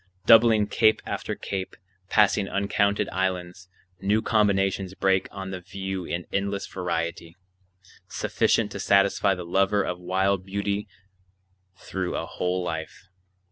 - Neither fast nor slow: No, slow, 125 wpm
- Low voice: Yes, very low, 95 Hz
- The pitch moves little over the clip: Yes, narrow, 1.6 semitones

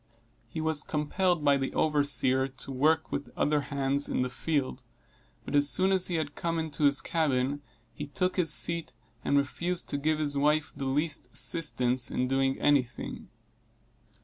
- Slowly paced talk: No, average, 175 wpm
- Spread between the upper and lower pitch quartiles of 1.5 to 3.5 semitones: Yes, average, 2.8 semitones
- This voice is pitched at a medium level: Yes, medium, 145 Hz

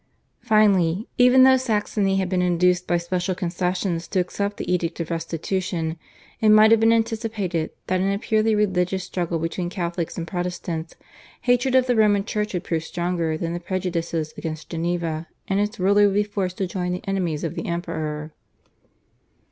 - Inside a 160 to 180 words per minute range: Yes, average, 175 wpm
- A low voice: No, medium, 180 Hz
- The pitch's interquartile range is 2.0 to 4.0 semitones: Yes, average, 3.4 semitones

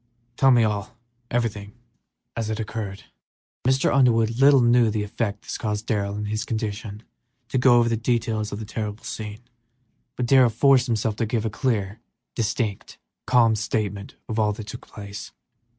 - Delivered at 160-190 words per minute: Yes, average, 170 wpm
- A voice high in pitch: No, low, 110 Hz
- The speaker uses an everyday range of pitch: No, narrow, 2.3 semitones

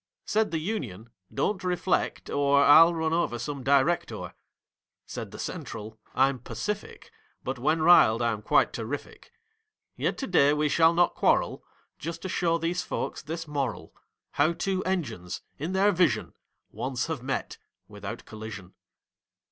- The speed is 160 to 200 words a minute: No, average, 140 wpm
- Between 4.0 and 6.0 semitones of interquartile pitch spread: Yes, wide, 5.4 semitones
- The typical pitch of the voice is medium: Yes, medium, 155 Hz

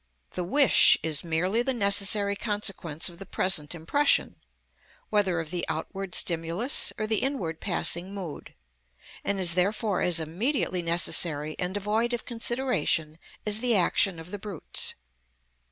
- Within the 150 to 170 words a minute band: No, average, 140 wpm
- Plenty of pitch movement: No, average, 4.2 semitones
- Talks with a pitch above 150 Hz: Yes, high, 190 Hz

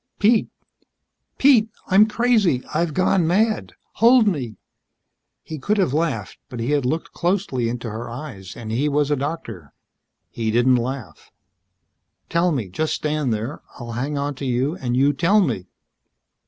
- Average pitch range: No, wide, 6.6 semitones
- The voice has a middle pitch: Yes, medium, 145 Hz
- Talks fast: No, average, 155 wpm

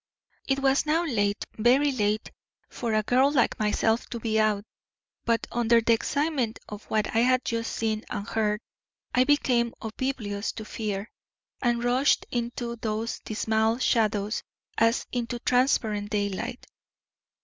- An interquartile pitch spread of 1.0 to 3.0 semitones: Yes, narrow, 2.5 semitones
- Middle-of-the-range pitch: No, high, 230 Hz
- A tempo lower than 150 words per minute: Yes, average, 140 wpm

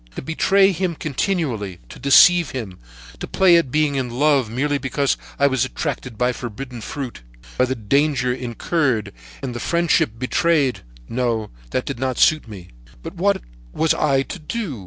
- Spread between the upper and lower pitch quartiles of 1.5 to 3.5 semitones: No, average, 4.1 semitones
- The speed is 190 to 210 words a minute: No, average, 165 wpm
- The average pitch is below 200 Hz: Yes, low, 135 Hz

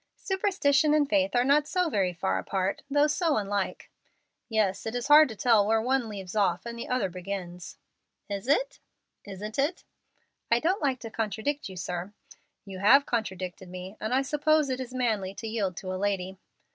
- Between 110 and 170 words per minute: No, average, 185 wpm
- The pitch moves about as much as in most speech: No, wide, 6.6 semitones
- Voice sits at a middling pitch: No, high, 220 Hz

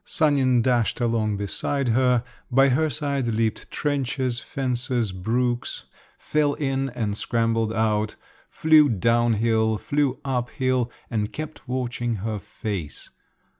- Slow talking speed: Yes, slow, 125 wpm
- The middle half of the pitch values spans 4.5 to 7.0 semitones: No, average, 3.2 semitones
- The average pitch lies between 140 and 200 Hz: No, low, 120 Hz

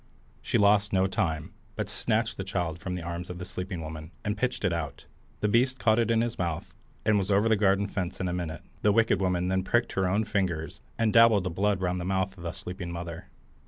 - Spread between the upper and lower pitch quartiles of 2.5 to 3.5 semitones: Yes, average, 2.9 semitones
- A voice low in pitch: Yes, very low, 95 Hz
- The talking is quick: Yes, fast, 235 wpm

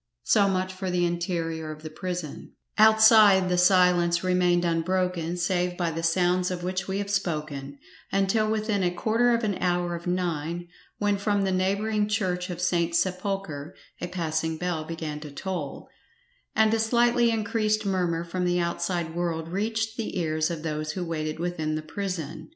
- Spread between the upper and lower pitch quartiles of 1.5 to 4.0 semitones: Yes, average, 3.0 semitones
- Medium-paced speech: Yes, average, 170 wpm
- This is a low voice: No, medium, 180 Hz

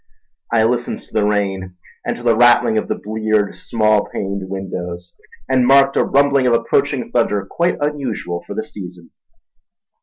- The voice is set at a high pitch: No, low, 110 Hz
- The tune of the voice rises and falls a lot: No, average, 4.2 semitones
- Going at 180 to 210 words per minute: No, average, 160 wpm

